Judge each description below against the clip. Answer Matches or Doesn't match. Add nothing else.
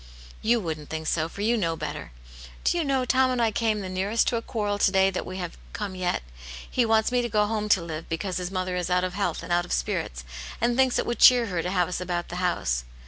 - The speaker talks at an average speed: Doesn't match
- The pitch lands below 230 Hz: Matches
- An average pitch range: Matches